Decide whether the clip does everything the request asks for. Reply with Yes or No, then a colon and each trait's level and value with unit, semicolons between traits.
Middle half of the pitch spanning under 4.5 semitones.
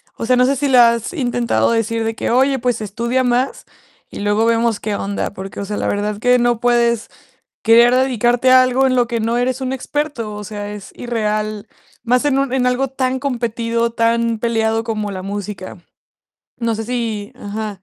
Yes: narrow, 2.6 semitones